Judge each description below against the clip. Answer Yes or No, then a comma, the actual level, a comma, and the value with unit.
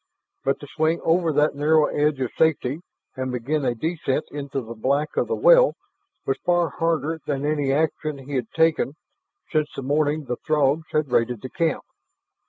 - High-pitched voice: No, medium, 150 Hz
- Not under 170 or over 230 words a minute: Yes, average, 180 wpm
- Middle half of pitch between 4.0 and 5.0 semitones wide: No, average, 2.8 semitones